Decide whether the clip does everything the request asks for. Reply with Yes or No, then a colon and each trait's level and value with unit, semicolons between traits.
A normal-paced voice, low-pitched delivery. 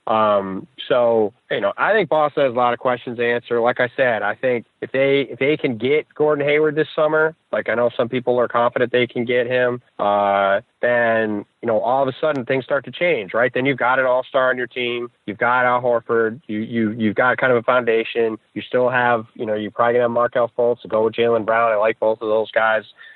No: fast, 245 wpm; low, 120 Hz